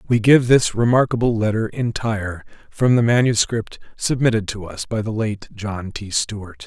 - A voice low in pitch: Yes, low, 110 Hz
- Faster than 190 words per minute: No, average, 160 wpm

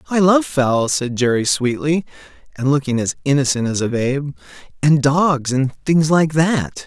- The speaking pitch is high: No, medium, 140 Hz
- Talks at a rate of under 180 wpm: Yes, average, 165 wpm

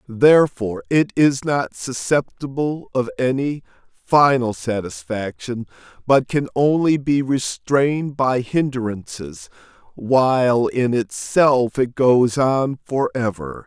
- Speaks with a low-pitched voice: Yes, low, 130 Hz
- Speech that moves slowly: Yes, slow, 105 wpm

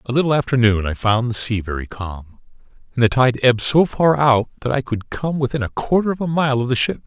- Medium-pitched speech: No, low, 125 Hz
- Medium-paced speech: No, fast, 255 wpm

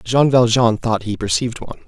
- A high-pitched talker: No, low, 115 Hz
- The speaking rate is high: No, average, 190 wpm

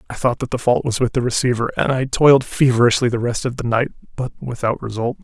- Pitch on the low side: Yes, low, 120 Hz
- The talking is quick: Yes, fast, 240 wpm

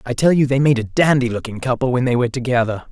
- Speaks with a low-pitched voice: Yes, low, 125 Hz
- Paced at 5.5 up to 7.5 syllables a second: Yes, 6.8 syllables/s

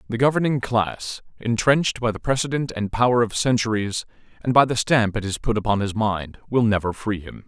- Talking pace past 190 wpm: Yes, average, 200 wpm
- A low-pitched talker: Yes, low, 115 Hz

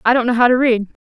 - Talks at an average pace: No, fast, 350 wpm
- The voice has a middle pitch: No, high, 240 Hz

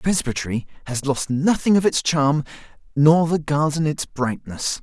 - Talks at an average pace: Yes, average, 160 wpm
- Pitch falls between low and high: Yes, medium, 145 Hz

